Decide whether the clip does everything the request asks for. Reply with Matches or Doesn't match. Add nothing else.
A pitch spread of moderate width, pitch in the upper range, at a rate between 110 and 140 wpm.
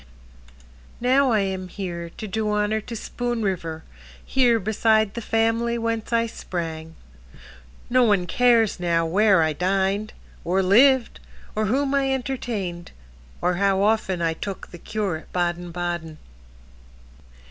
Matches